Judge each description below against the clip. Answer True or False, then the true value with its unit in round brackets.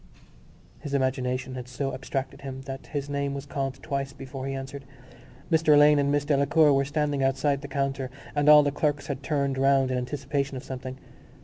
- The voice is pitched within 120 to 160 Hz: True (140 Hz)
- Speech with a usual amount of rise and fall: False (1.4 semitones)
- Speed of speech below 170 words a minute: False (190 wpm)